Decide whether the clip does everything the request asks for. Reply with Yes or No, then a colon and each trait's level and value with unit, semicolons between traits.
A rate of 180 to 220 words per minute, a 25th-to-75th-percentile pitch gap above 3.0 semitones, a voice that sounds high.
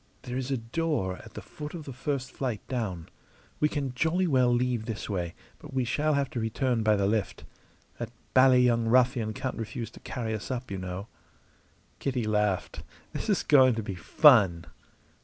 No: average, 190 wpm; average, 3.7 semitones; low, 120 Hz